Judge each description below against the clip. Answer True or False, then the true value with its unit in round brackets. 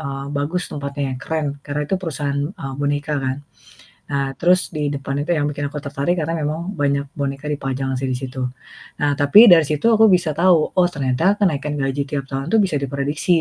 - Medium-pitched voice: True (145 Hz)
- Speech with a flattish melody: True (2.1 semitones)